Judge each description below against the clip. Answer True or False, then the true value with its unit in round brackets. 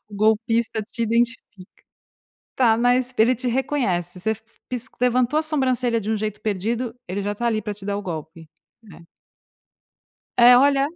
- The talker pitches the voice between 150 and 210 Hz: False (230 Hz)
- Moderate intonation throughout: True (3.3 semitones)